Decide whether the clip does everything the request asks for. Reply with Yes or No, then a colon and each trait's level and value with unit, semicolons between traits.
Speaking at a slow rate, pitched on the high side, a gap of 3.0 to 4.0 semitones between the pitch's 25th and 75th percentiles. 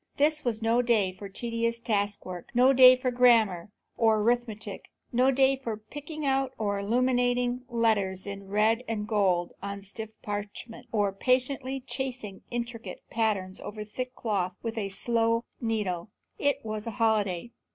No: average, 150 wpm; high, 225 Hz; average, 3.4 semitones